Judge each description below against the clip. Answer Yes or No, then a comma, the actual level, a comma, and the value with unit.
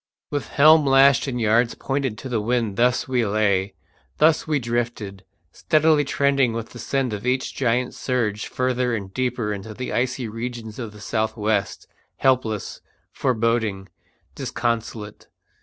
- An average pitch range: Yes, average, 3.1 semitones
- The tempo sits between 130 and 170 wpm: Yes, average, 145 wpm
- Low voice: Yes, low, 120 Hz